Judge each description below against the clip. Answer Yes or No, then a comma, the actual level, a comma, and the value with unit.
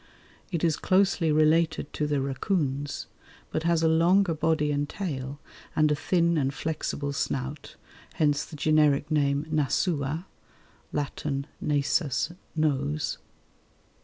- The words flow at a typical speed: No, slow, 120 wpm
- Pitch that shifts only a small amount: Yes, narrow, 2.3 semitones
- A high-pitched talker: No, medium, 150 Hz